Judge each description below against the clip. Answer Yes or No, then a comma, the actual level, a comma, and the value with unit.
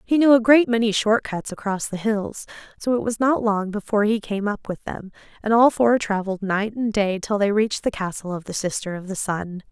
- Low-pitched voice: No, high, 210 Hz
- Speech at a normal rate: No, fast, 240 wpm